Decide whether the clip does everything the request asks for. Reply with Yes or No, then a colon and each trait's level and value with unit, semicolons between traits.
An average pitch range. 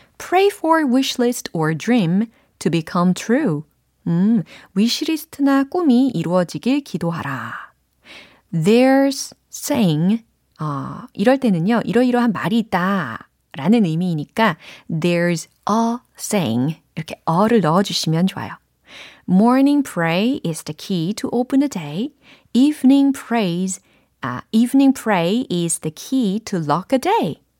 No: wide, 6.8 semitones